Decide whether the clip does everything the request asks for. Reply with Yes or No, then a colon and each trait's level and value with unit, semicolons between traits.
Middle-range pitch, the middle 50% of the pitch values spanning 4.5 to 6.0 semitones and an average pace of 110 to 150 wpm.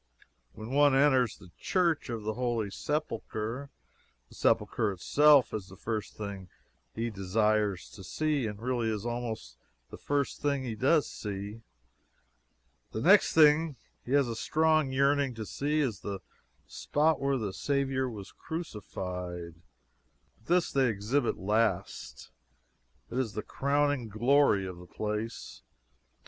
No: low, 120 Hz; average, 5.3 semitones; average, 140 wpm